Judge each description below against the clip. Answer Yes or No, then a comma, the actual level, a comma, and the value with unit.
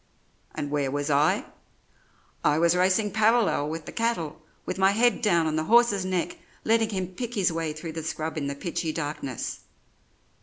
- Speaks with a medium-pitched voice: Yes, medium, 170 Hz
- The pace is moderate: Yes, average, 180 wpm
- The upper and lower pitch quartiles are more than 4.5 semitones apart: Yes, average, 5.2 semitones